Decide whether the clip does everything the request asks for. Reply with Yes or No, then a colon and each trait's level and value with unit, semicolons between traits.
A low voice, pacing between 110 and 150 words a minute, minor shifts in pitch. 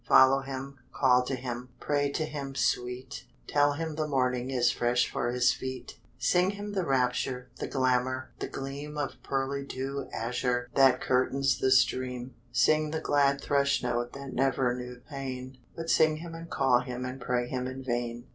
No: low, 130 Hz; average, 175 wpm; narrow, 2.0 semitones